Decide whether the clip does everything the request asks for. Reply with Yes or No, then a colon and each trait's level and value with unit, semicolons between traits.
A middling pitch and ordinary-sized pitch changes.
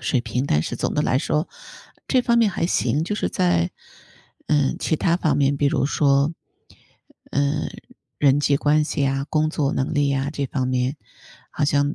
No: medium, 145 Hz; narrow, 2.1 semitones